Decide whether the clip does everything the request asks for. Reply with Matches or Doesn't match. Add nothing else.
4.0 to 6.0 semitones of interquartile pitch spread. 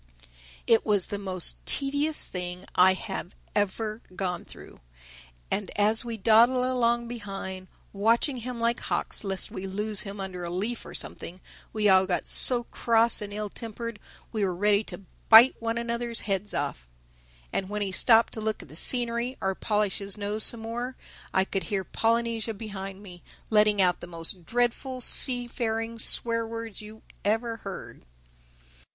Doesn't match